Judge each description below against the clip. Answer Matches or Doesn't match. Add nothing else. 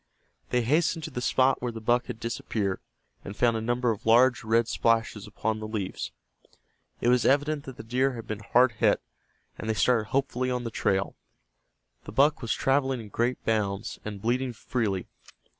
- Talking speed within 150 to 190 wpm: Matches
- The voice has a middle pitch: Doesn't match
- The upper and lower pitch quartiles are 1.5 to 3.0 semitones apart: Matches